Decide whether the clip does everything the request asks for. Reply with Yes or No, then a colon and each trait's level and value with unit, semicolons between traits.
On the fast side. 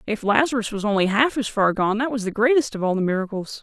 Yes: fast, 265 wpm